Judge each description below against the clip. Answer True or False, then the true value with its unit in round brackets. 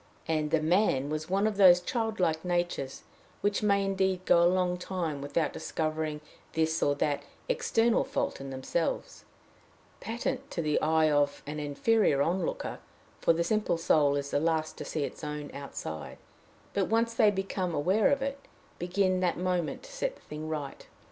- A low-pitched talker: False (170 Hz)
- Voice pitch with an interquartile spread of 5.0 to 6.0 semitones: False (4.5 semitones)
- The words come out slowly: False (175 wpm)